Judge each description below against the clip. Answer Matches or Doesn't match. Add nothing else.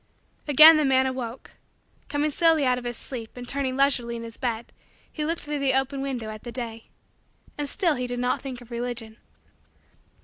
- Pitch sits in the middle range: Doesn't match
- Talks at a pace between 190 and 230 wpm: Matches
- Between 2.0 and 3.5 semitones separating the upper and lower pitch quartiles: Matches